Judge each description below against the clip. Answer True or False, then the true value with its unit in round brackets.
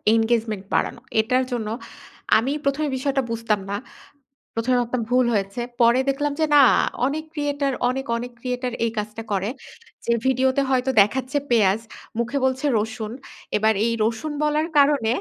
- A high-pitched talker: True (245 Hz)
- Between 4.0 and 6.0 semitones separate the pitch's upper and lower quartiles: False (3.5 semitones)